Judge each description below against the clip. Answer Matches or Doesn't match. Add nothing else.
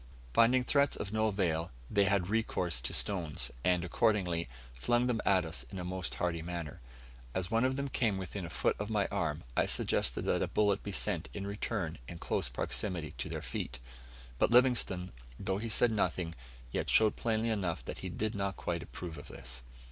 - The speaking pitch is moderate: Doesn't match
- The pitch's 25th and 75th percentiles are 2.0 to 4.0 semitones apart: Doesn't match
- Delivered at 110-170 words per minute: Doesn't match